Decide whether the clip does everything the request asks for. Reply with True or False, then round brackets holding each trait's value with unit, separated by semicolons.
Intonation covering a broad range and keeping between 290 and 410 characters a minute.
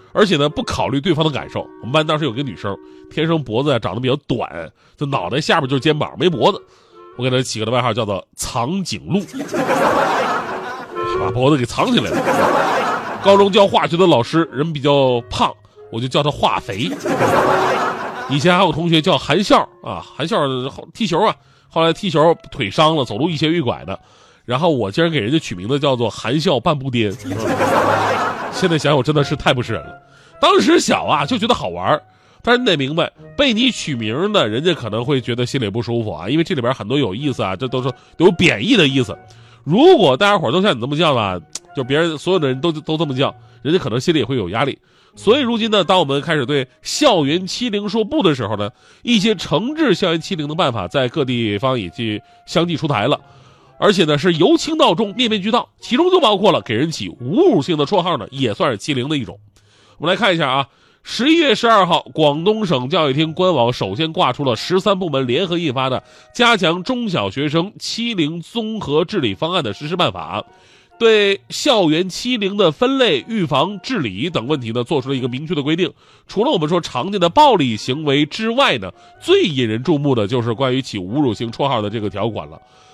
True (6.8 semitones; 305 characters per minute)